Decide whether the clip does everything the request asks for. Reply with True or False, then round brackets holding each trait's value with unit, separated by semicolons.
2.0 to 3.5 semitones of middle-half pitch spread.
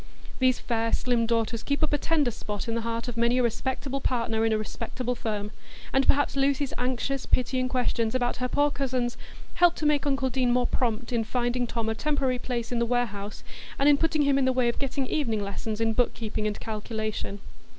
True (2.9 semitones)